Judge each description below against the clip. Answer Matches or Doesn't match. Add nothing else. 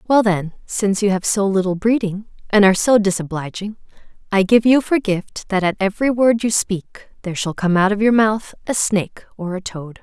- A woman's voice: Matches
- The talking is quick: Matches